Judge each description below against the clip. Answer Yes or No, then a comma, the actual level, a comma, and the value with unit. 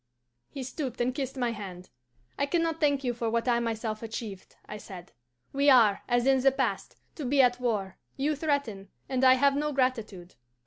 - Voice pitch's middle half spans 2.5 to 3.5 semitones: No, average, 3.9 semitones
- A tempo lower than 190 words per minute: No, average, 195 wpm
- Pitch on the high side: Yes, very high, 250 Hz